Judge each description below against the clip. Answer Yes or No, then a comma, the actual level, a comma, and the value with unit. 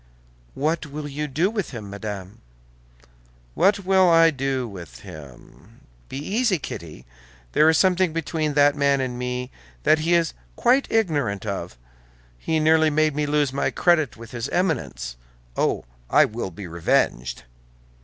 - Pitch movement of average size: No, wide, 7.0 semitones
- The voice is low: No, medium, 145 Hz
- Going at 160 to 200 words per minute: No, average, 150 wpm